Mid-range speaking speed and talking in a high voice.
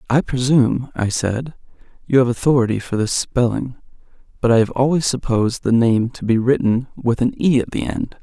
No: average, 190 wpm; low, 125 Hz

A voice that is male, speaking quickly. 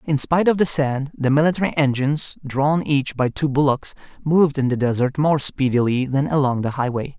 No: male; average, 190 wpm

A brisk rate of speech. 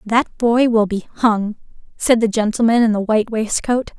No: average, 180 wpm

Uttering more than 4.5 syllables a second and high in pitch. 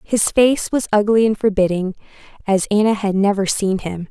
Yes: 5.0 syllables/s; high, 205 Hz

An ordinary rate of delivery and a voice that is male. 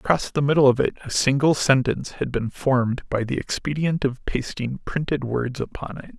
Yes: average, 195 wpm; male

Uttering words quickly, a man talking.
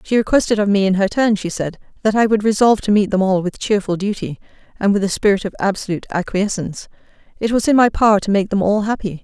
No: fast, 240 wpm; female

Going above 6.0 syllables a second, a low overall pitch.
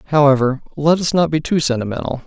No: 6.4 syllables/s; medium, 145 Hz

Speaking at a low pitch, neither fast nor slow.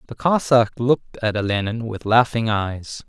Yes: low, 115 Hz; average, 155 wpm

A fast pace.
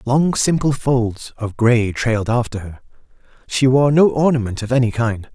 No: average, 170 wpm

